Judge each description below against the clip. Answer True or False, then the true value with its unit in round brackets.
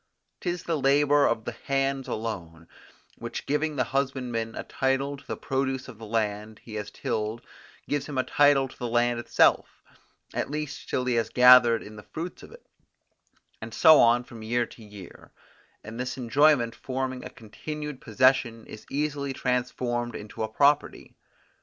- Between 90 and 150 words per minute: False (170 wpm)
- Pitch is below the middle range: True (125 Hz)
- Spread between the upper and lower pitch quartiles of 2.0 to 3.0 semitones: False (3.6 semitones)